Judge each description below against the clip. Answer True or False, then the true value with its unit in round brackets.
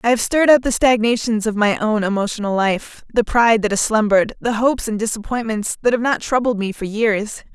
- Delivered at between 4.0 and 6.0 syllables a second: True (5.8 syllables/s)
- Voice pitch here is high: True (220 Hz)